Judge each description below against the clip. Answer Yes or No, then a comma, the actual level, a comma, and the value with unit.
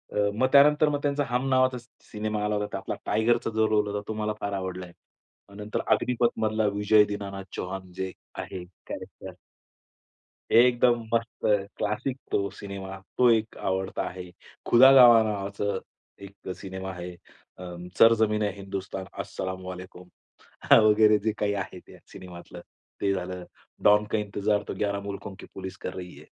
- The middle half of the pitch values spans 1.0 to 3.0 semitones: Yes, average, 2.7 semitones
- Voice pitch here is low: Yes, low, 105 Hz